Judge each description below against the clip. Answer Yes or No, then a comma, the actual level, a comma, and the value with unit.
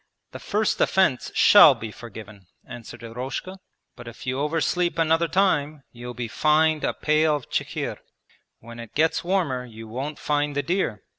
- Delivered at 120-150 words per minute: No, average, 160 wpm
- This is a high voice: No, medium, 145 Hz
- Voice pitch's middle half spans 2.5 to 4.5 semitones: No, average, 5.3 semitones